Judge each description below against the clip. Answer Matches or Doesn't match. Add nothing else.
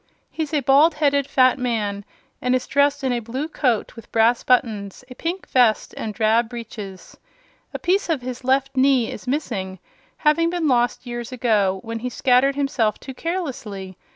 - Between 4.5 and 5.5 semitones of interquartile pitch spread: Doesn't match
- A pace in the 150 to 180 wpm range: Matches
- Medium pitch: Doesn't match